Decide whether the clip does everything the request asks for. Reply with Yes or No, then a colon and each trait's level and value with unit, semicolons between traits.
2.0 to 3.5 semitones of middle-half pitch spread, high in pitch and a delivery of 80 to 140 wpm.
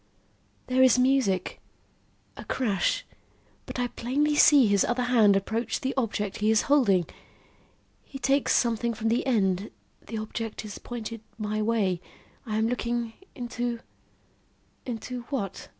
Yes: average, 2.9 semitones; high, 230 Hz; slow, 135 wpm